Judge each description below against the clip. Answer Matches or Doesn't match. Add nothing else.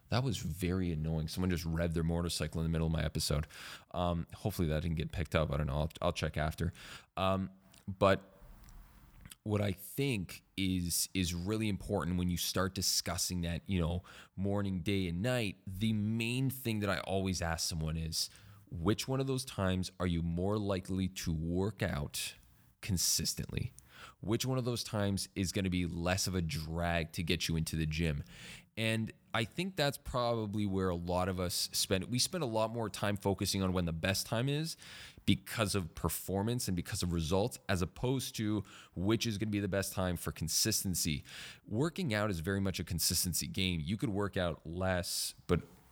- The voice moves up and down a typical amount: Matches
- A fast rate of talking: Doesn't match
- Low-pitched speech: Matches